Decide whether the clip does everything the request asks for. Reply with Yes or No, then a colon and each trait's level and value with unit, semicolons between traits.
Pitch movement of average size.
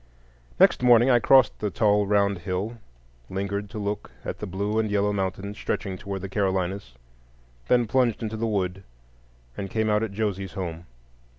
No: narrow, 2.2 semitones